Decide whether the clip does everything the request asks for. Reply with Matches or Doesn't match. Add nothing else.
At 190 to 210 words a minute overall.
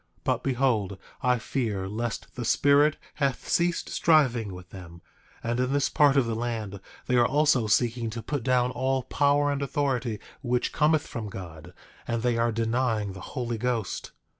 Doesn't match